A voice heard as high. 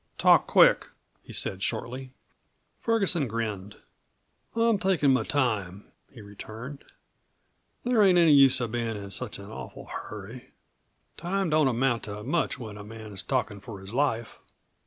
No: low, 120 Hz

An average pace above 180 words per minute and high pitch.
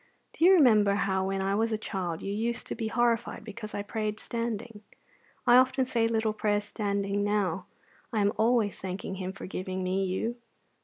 Yes: average, 190 wpm; high, 210 Hz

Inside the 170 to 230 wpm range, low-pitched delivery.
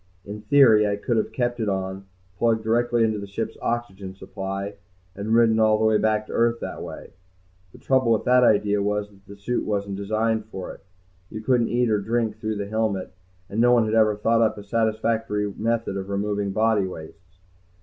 Yes: average, 200 wpm; low, 110 Hz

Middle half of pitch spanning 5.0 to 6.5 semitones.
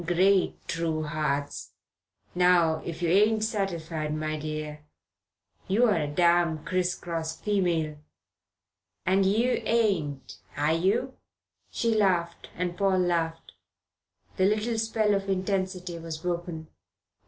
No: average, 3.5 semitones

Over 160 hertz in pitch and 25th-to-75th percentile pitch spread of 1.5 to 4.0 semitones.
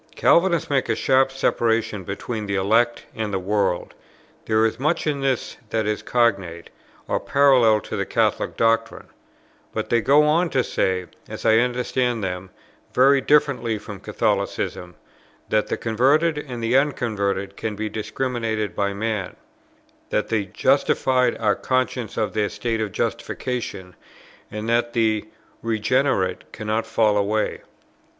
No: low, 115 Hz; average, 3.5 semitones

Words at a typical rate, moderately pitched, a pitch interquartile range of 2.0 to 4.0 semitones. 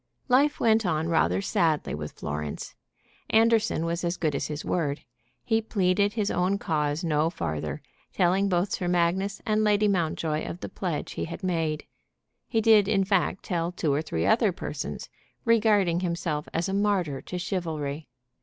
No: average, 165 wpm; medium, 175 Hz; average, 4.6 semitones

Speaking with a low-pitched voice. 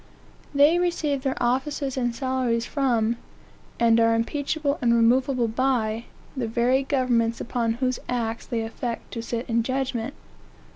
No: high, 245 Hz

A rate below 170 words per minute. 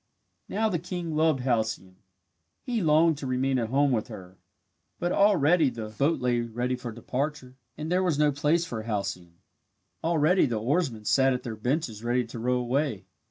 No: average, 175 wpm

